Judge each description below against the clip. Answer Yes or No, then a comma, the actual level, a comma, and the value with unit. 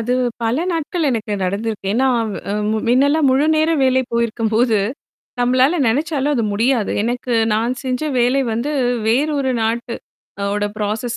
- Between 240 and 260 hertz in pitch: Yes, high, 245 Hz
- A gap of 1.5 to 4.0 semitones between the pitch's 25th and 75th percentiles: Yes, average, 3.6 semitones